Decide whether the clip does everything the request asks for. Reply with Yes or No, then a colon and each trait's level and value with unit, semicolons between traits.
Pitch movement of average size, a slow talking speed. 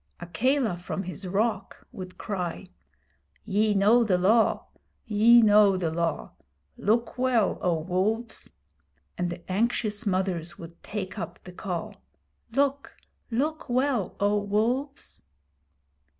Yes: average, 4.3 semitones; slow, 120 wpm